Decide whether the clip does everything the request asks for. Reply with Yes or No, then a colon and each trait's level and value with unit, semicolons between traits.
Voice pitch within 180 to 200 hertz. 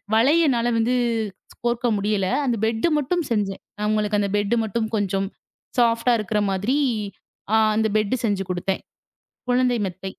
No: high, 220 Hz